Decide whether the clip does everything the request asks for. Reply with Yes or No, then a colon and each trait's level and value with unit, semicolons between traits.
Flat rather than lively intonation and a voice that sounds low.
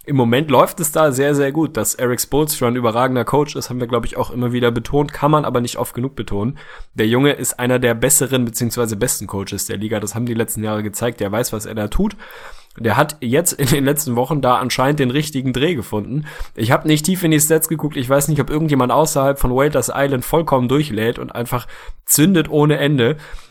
No: average, 3.8 semitones; low, 130 Hz